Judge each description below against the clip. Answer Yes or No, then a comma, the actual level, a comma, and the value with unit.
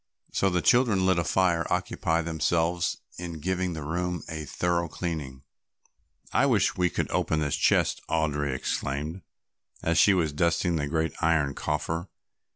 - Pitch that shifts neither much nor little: No, narrow, 2.3 semitones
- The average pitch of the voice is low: Yes, very low, 85 Hz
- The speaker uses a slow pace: No, average, 160 wpm